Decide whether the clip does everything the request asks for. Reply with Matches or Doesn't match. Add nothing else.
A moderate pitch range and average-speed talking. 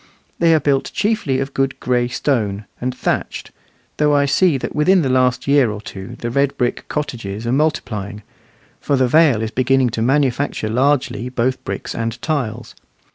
Matches